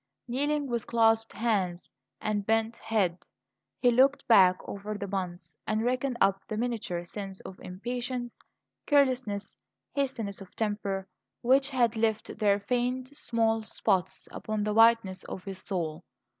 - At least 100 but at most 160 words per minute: Yes, average, 140 wpm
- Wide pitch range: No, average, 3.7 semitones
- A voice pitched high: Yes, high, 220 Hz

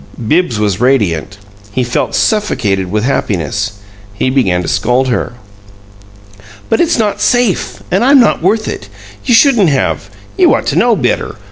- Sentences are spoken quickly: No, average, 155 wpm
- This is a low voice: Yes, low, 130 Hz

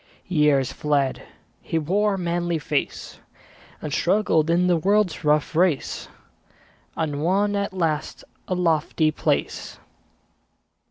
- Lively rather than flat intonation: No, average, 3.4 semitones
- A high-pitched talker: No, medium, 165 Hz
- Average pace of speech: No, slow, 115 wpm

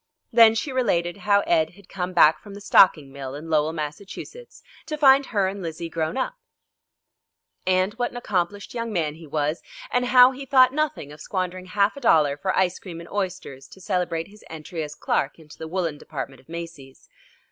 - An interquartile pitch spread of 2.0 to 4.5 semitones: No, average, 4.9 semitones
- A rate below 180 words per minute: No, average, 195 wpm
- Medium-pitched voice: Yes, medium, 180 Hz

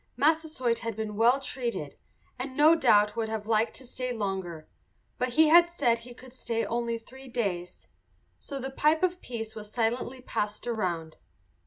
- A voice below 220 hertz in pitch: No, high, 235 Hz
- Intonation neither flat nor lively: Yes, average, 3.5 semitones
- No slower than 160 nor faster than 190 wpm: Yes, average, 170 wpm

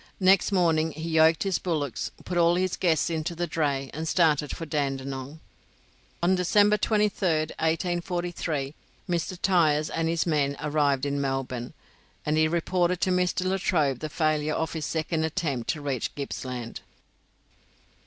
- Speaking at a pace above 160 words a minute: No, average, 145 wpm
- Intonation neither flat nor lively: Yes, average, 3.2 semitones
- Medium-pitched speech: Yes, medium, 160 Hz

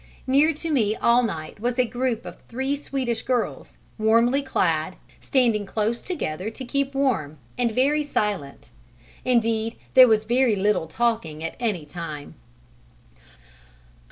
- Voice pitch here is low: No, high, 230 Hz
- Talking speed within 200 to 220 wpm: No, slow, 135 wpm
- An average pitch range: Yes, average, 4.2 semitones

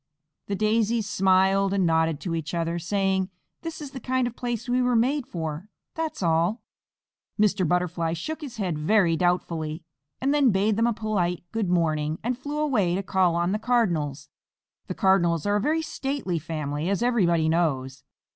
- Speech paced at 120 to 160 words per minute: No, average, 175 wpm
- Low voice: No, high, 190 Hz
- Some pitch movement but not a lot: No, wide, 5.9 semitones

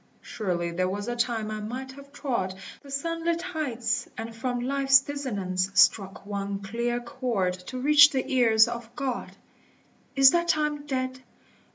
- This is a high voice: Yes, high, 245 Hz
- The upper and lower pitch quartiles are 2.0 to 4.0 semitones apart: No, average, 4.5 semitones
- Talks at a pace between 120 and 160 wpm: Yes, average, 155 wpm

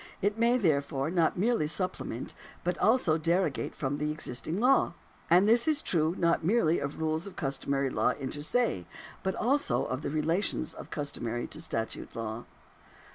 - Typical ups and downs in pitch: No, wide, 5.7 semitones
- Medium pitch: Yes, medium, 160 Hz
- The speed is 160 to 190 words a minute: Yes, average, 170 wpm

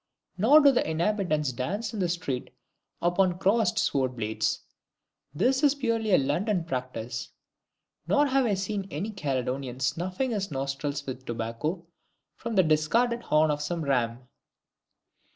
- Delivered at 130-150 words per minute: Yes, average, 140 wpm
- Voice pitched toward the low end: No, medium, 170 Hz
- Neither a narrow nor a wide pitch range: No, wide, 7.8 semitones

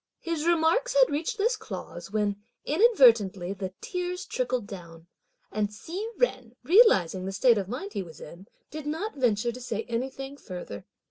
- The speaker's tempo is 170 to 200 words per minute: No, average, 160 wpm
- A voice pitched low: No, high, 245 Hz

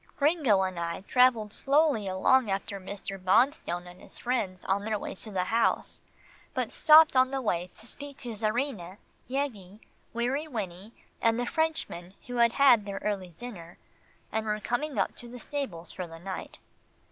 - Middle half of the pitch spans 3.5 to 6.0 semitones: Yes, wide, 5.4 semitones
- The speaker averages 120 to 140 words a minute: No, average, 170 wpm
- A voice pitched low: No, high, 220 Hz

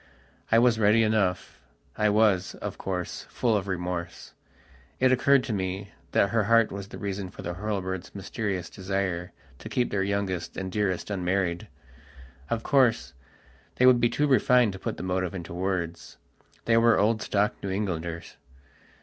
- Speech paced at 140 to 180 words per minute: Yes, average, 165 wpm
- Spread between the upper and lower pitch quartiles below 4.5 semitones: Yes, average, 3.3 semitones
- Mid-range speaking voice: No, low, 100 Hz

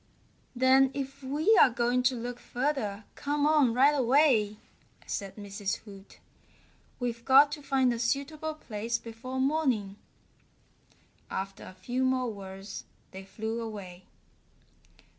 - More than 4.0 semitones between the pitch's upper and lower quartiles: Yes, average, 4.5 semitones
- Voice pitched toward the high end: Yes, high, 245 Hz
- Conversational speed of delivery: No, slow, 125 wpm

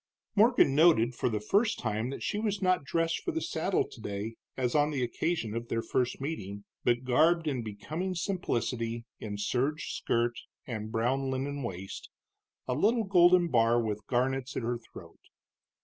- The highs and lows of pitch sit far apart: Yes, wide, 6.3 semitones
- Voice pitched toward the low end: Yes, low, 130 Hz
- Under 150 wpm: No, average, 165 wpm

